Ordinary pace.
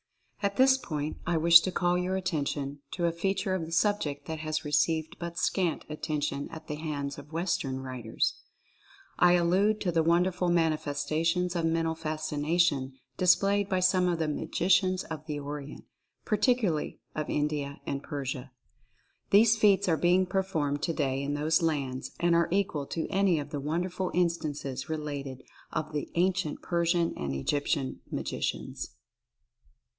Yes: average, 160 wpm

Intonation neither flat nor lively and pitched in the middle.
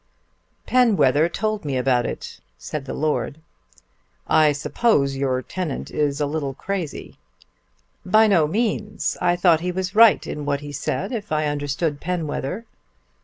Yes: average, 4.9 semitones; medium, 155 Hz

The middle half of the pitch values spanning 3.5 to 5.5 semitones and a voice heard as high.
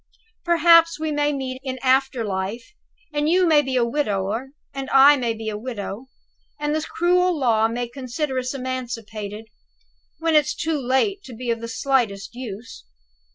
Yes: average, 4.4 semitones; very high, 260 Hz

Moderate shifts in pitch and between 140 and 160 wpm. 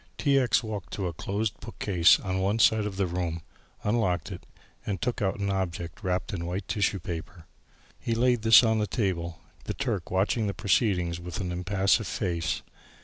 No: average, 3.5 semitones; average, 180 wpm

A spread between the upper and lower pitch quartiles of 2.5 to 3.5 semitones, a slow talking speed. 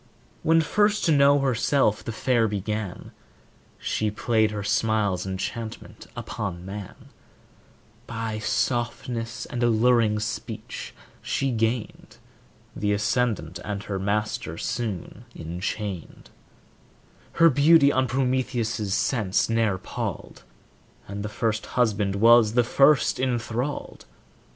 Yes: average, 3.1 semitones; slow, 110 wpm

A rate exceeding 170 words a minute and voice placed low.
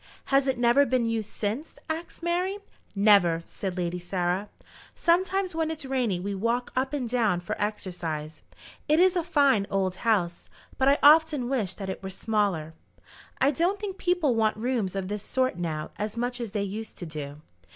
No: average, 185 wpm; high, 225 Hz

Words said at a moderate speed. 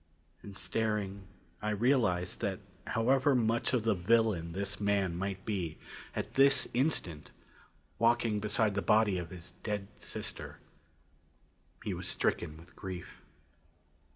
No: slow, 125 wpm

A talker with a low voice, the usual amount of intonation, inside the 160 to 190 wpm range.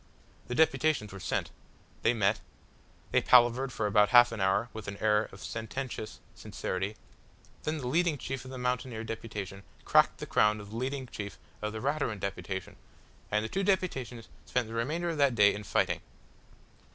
Yes: low, 115 Hz; average, 3.9 semitones; average, 175 wpm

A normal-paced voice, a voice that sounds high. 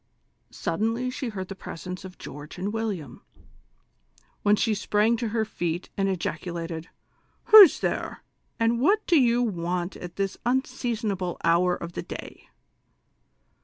Yes: average, 145 wpm; high, 200 Hz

